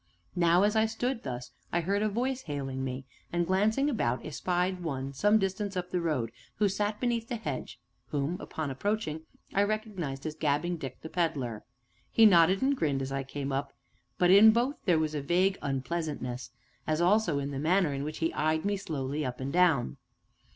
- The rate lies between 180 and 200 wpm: Yes, average, 195 wpm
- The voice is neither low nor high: Yes, medium, 170 Hz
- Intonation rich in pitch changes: Yes, wide, 6.5 semitones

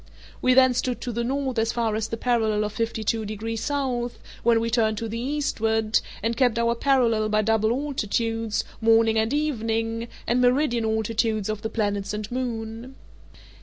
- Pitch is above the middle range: Yes, high, 225 Hz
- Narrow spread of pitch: Yes, narrow, 1.9 semitones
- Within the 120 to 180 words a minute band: Yes, average, 175 wpm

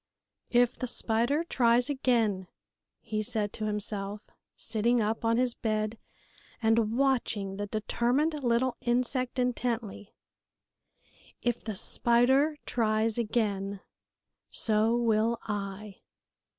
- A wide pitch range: No, narrow, 2.4 semitones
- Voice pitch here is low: No, high, 230 Hz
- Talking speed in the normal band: No, slow, 105 wpm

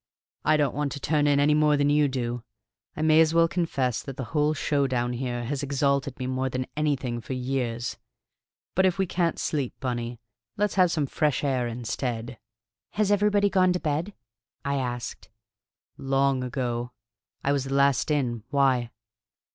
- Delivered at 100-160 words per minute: No, average, 175 wpm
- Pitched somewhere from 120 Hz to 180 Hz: Yes, medium, 140 Hz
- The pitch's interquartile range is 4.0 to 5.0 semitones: No, average, 3.3 semitones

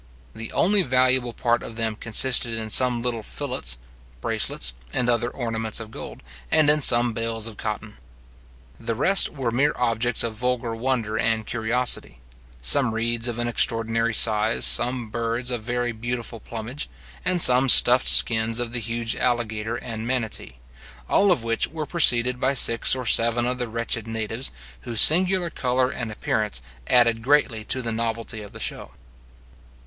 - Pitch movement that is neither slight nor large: No, narrow, 1.9 semitones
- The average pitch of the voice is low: Yes, low, 120 Hz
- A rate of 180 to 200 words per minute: No, average, 165 wpm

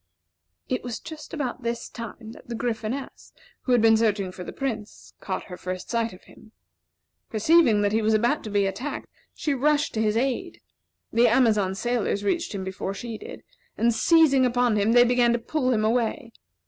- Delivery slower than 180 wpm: No, average, 190 wpm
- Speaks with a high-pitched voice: Yes, high, 230 Hz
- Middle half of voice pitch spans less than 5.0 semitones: Yes, average, 2.9 semitones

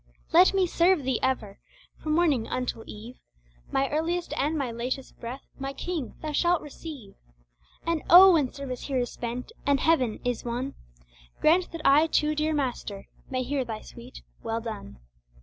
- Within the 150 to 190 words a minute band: Yes, average, 165 wpm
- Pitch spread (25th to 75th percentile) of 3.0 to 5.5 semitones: Yes, average, 4.6 semitones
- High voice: Yes, very high, 275 Hz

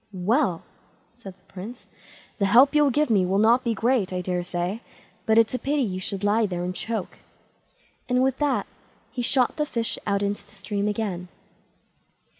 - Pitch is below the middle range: No, high, 215 Hz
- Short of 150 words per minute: No, average, 180 wpm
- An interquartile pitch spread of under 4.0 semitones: No, average, 4.6 semitones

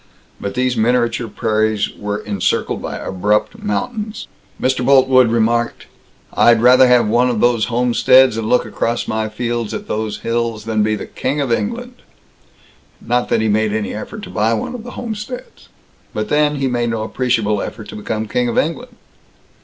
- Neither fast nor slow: Yes, average, 170 wpm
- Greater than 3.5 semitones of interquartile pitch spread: No, average, 3.2 semitones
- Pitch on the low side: Yes, low, 120 Hz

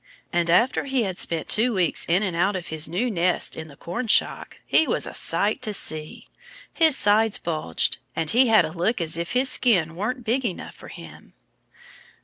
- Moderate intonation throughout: No, wide, 5.7 semitones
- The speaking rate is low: No, average, 195 wpm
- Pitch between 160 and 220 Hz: Yes, high, 190 Hz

